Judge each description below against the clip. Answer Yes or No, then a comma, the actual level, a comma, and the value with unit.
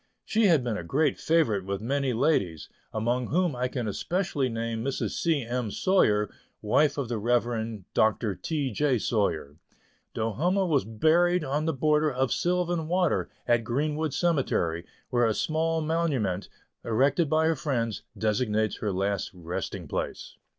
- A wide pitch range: Yes, wide, 6.2 semitones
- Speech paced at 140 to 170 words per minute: Yes, average, 155 wpm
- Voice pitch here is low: Yes, low, 130 Hz